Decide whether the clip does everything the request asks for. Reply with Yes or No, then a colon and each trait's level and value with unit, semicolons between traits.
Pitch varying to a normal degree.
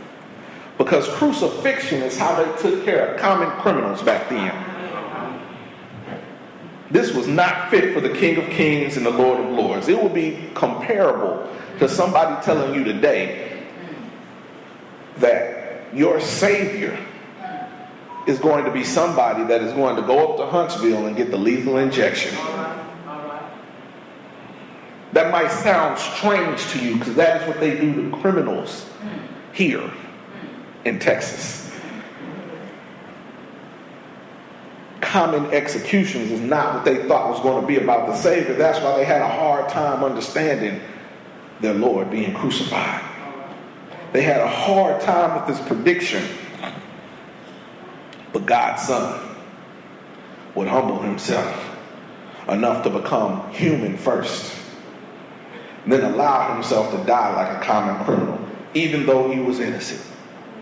No: wide, 6.2 semitones